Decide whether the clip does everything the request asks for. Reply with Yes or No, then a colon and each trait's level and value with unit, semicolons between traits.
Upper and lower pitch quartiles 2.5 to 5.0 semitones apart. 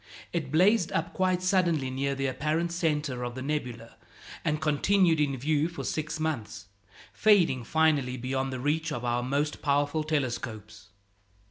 Yes: average, 3.7 semitones